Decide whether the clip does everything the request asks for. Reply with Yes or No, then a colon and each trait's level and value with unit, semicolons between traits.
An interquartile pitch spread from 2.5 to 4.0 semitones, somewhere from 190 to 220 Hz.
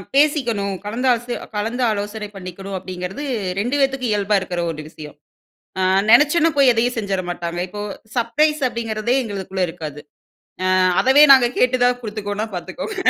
No: average, 4.7 semitones; high, 215 Hz